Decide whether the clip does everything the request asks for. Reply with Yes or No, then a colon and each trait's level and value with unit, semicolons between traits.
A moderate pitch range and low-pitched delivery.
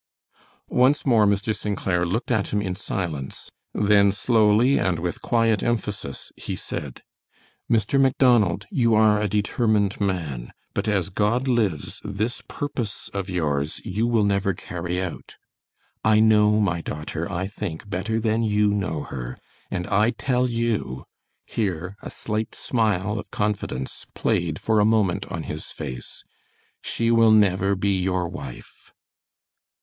Yes: average, 3.4 semitones; low, 105 Hz